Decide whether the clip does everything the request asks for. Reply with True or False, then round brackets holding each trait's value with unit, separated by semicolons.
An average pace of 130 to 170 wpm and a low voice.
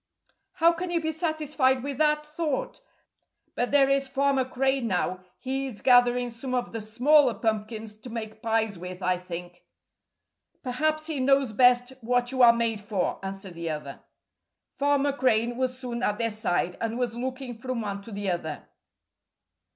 False (165 wpm; 245 Hz)